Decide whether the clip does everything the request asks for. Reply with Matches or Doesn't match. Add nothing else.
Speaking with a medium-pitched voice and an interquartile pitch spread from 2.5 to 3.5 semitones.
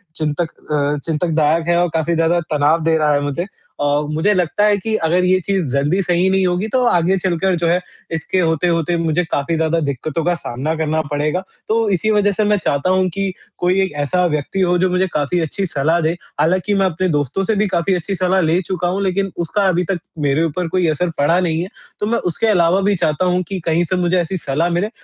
Matches